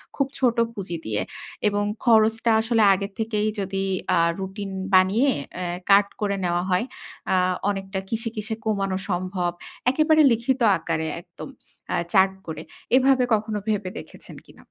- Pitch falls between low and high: No, high, 205 Hz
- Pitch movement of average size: Yes, average, 3.2 semitones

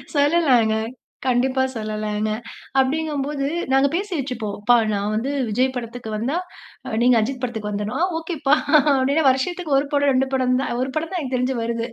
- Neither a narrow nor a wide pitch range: Yes, average, 3.7 semitones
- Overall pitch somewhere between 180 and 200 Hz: No, very high, 260 Hz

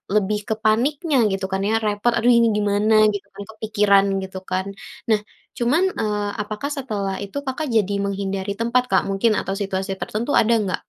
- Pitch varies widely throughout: No, average, 2.9 semitones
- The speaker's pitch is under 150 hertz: No, high, 210 Hz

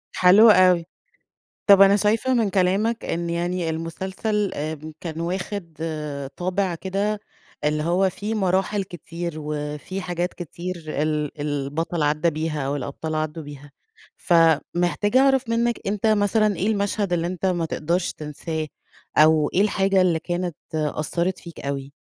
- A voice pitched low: No, medium, 175 Hz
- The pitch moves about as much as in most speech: Yes, average, 3.9 semitones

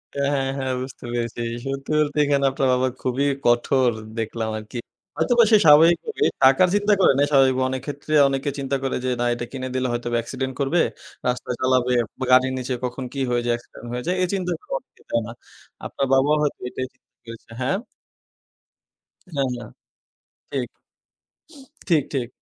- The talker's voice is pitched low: Yes, low, 130 Hz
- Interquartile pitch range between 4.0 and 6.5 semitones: No, narrow, 2.5 semitones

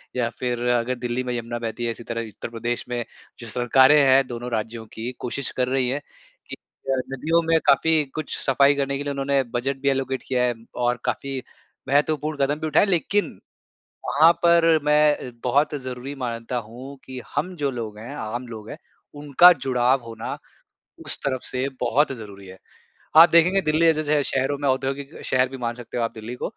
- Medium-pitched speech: No, low, 130 Hz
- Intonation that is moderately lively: Yes, average, 3.2 semitones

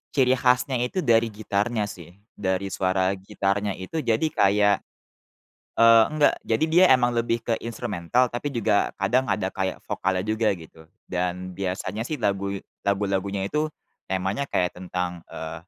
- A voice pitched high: No, low, 100 Hz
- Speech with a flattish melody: No, average, 4.2 semitones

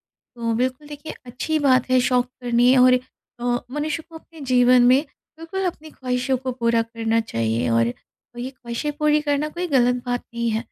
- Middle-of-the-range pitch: No, very high, 255 Hz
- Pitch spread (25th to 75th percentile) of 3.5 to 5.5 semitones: Yes, average, 3.8 semitones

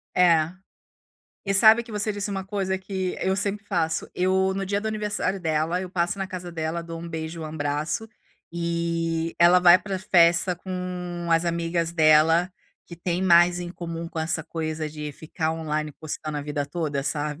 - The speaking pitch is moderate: Yes, medium, 170 Hz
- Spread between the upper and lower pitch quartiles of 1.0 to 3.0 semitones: Yes, average, 2.7 semitones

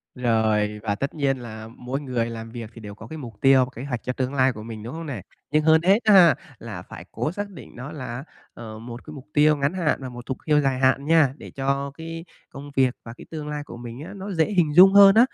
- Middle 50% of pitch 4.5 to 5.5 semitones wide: Yes, average, 4.8 semitones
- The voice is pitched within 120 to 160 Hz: Yes, low, 135 Hz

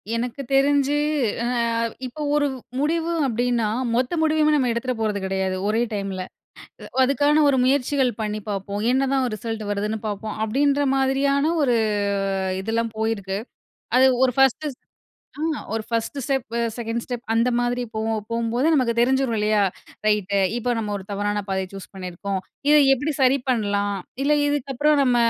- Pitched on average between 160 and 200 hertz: No, high, 240 Hz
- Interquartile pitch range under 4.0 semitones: No, average, 4.3 semitones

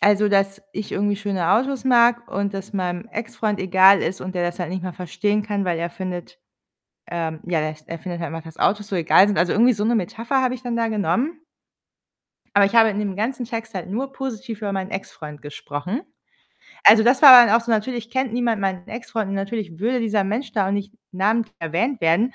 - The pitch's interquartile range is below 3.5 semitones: No, average, 4.0 semitones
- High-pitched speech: Yes, high, 205 Hz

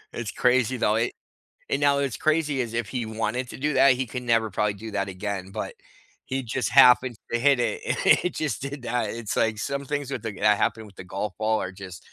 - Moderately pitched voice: No, low, 120 Hz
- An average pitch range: Yes, average, 3.9 semitones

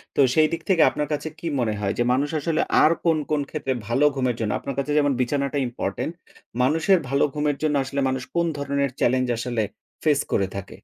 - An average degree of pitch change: Yes, average, 3.2 semitones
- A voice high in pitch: No, medium, 140 Hz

